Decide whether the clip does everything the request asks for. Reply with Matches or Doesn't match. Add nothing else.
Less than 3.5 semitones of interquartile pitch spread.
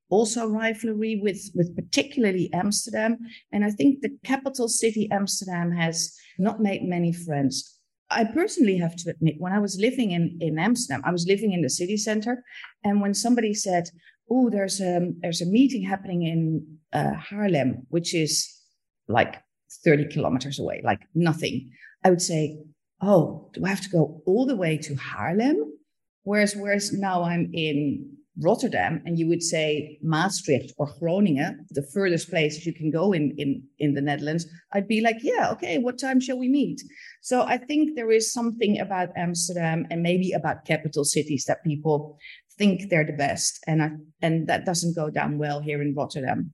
Doesn't match